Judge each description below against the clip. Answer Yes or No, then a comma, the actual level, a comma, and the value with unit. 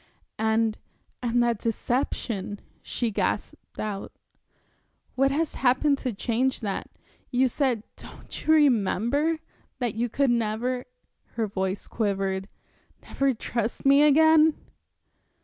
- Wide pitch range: No, average, 4.1 semitones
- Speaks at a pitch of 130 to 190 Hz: No, high, 240 Hz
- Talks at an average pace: No, slow, 115 wpm